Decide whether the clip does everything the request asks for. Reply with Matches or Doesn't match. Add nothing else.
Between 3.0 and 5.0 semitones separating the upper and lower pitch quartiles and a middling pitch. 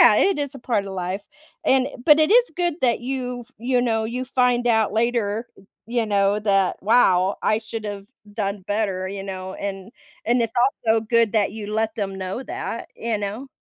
Doesn't match